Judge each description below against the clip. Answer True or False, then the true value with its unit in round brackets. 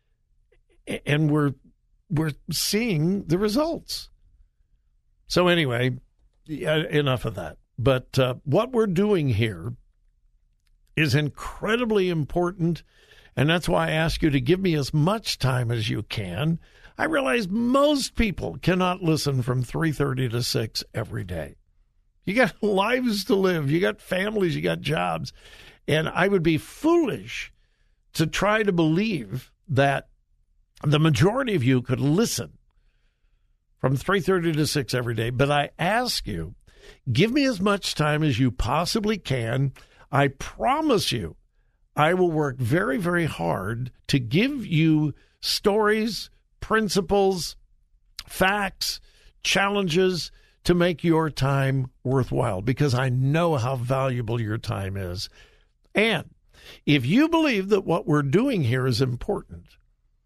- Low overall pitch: False (150 Hz)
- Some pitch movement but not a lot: False (6.7 semitones)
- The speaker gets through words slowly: True (130 wpm)